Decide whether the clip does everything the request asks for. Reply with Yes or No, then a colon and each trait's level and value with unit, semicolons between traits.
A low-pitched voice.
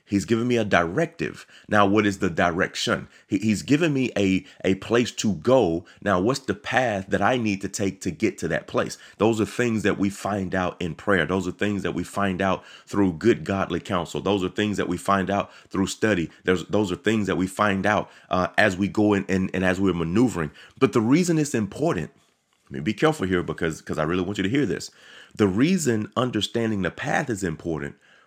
Yes: low, 100 Hz